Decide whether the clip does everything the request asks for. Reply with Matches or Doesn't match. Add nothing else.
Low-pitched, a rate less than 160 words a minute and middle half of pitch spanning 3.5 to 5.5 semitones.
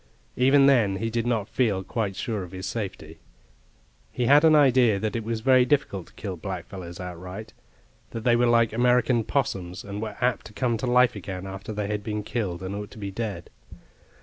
Doesn't match